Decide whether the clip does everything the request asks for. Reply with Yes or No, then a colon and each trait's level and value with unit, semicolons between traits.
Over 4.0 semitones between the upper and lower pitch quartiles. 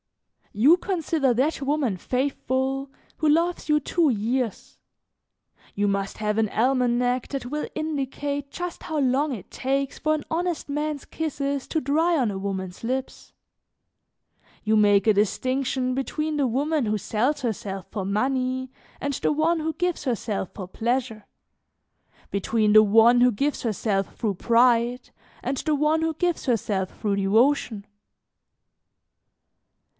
Yes: wide, 5.4 semitones